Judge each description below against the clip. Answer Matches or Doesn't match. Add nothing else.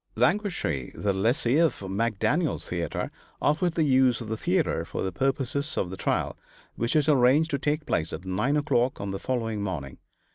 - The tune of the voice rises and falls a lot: Matches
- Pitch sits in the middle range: Doesn't match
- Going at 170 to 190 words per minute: Matches